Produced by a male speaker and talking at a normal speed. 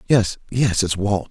Yes: male; average, 185 wpm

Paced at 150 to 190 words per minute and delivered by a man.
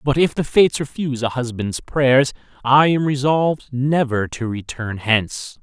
Yes: average, 160 wpm; male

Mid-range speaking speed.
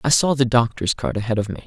No: fast, 290 wpm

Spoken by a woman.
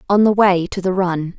Yes: female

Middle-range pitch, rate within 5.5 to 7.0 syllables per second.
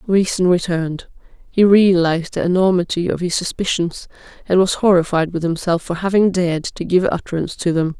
Yes: medium, 175 Hz; 5.7 syllables/s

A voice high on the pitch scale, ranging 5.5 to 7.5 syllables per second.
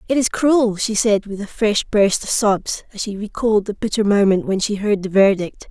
No: high, 210 Hz; 5.0 syllables/s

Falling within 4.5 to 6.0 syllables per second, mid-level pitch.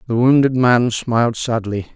No: 4.7 syllables/s; low, 120 Hz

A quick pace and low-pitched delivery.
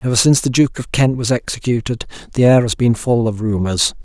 Yes: fast, 225 wpm; low, 120 Hz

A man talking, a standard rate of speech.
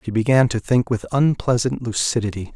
Yes: male; average, 165 wpm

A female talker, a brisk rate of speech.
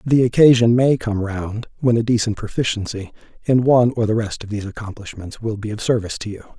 No: male; fast, 210 wpm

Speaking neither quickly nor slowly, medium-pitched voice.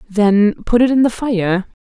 No: average, 195 wpm; high, 220 Hz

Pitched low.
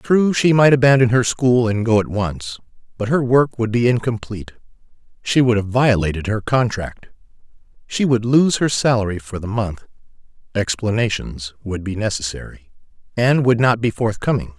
Yes: low, 115 Hz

